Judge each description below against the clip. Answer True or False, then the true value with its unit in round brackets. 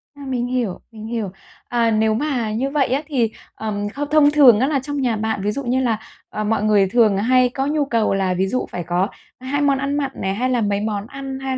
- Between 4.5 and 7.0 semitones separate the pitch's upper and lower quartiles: False (4.1 semitones)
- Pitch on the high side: True (240 Hz)